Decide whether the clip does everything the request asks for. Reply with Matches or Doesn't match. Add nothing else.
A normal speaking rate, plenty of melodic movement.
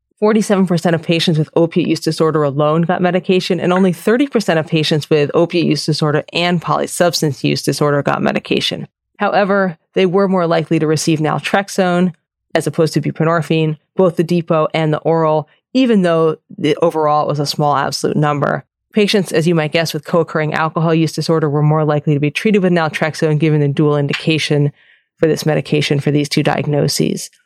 Doesn't match